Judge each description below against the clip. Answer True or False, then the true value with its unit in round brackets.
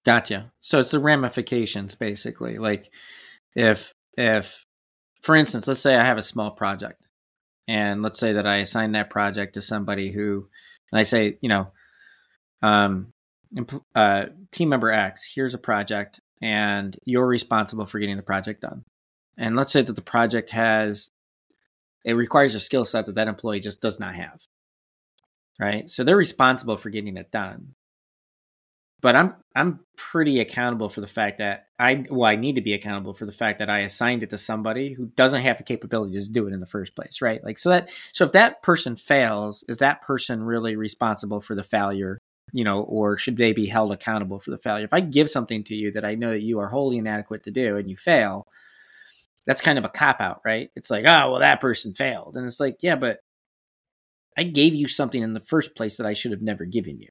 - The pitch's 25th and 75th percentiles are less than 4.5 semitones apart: True (3.2 semitones)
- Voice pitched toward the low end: True (110 Hz)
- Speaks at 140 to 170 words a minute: False (205 wpm)